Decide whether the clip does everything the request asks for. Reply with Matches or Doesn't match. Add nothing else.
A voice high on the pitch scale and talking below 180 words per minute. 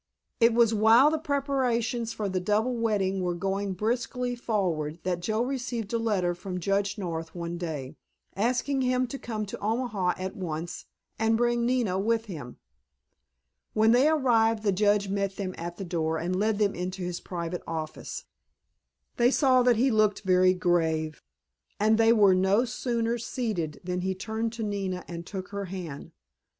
Matches